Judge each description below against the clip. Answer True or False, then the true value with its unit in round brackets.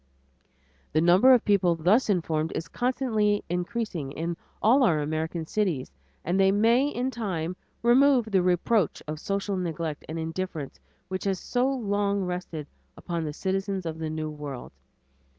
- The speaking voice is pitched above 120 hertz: True (185 Hz)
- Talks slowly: False (150 wpm)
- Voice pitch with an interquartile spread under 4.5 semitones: False (4.9 semitones)